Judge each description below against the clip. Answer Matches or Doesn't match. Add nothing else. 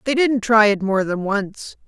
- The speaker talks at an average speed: Doesn't match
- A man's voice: Doesn't match